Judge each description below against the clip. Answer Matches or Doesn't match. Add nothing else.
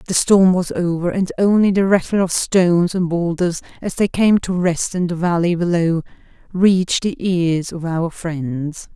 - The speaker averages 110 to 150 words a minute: Doesn't match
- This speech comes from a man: Doesn't match